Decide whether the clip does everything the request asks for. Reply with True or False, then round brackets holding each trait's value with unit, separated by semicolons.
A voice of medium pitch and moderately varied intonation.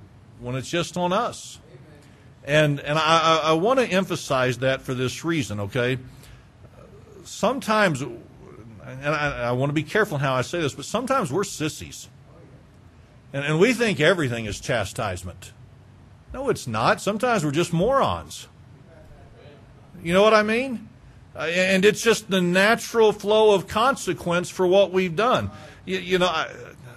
False (155 Hz; 7.2 semitones)